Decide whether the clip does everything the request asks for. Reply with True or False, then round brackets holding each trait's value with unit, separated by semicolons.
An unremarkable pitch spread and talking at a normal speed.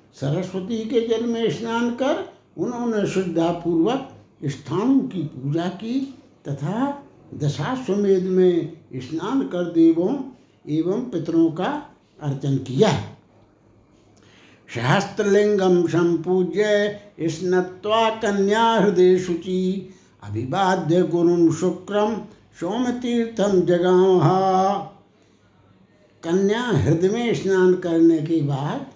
False (4.2 semitones; 85 wpm)